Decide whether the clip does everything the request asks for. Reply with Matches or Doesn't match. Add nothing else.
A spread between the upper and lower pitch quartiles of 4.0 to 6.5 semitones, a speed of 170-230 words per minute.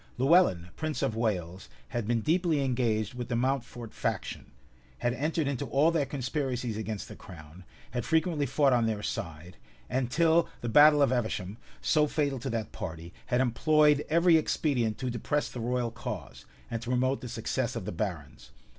Matches